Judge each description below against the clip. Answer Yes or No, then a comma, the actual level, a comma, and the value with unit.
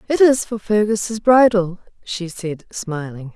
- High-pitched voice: Yes, high, 200 Hz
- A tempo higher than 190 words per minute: No, average, 145 wpm